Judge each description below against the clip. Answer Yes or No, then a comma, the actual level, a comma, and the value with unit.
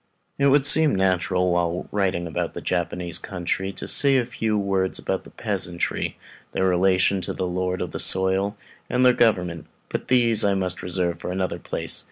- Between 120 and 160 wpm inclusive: No, average, 185 wpm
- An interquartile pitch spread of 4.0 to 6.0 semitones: No, average, 2.8 semitones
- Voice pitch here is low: Yes, very low, 95 Hz